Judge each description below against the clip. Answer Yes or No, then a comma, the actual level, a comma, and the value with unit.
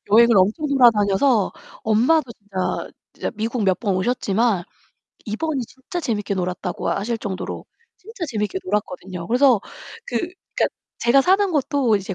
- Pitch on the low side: No, high, 225 Hz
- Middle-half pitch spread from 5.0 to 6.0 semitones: Yes, wide, 5.4 semitones